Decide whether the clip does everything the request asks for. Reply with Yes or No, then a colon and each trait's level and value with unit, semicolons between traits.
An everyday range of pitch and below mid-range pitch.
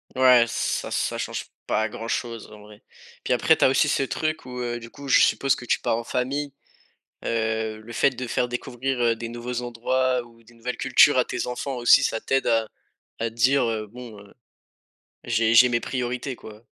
No: narrow, 1.9 semitones; low, 120 Hz